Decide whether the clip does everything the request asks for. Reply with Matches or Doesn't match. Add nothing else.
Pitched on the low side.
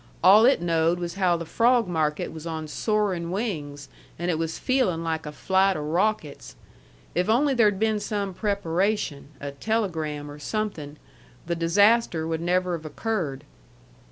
Doesn't match